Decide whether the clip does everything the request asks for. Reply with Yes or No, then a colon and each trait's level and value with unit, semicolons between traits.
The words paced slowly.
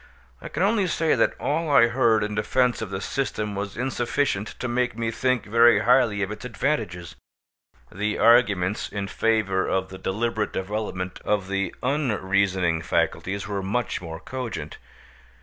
No: average, 155 wpm